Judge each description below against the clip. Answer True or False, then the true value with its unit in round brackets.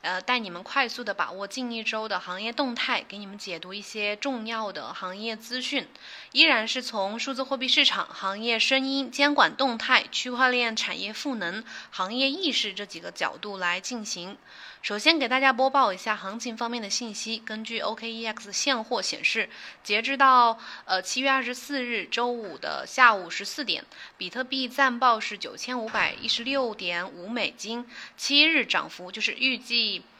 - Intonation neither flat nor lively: True (4.1 semitones)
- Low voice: False (230 Hz)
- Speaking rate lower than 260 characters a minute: False (270 characters per minute)